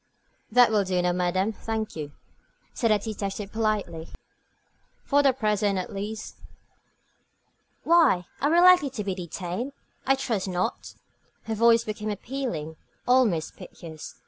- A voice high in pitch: Yes, high, 215 Hz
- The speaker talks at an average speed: No, slow, 130 wpm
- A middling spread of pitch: Yes, average, 4.6 semitones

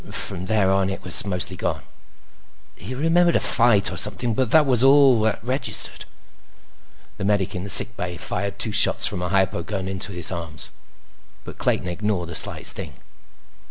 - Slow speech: No, average, 180 wpm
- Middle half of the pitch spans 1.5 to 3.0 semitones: No, average, 4.6 semitones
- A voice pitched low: Yes, low, 100 Hz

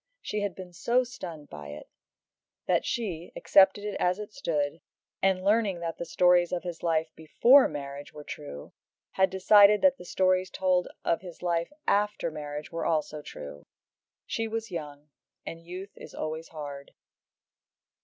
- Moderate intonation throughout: Yes, average, 4.3 semitones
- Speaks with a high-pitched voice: No, medium, 175 Hz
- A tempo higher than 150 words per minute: Yes, average, 160 wpm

